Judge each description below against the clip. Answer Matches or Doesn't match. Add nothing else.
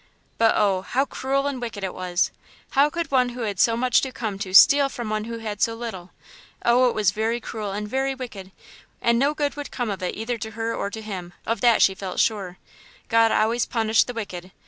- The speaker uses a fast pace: Matches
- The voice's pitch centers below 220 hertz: Doesn't match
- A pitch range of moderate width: Matches